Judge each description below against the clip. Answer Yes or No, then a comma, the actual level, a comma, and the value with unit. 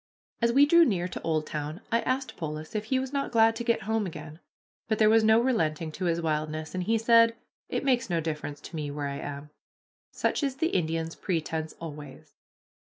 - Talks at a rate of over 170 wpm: Yes, fast, 205 wpm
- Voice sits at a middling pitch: Yes, medium, 175 Hz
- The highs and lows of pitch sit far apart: Yes, wide, 6.8 semitones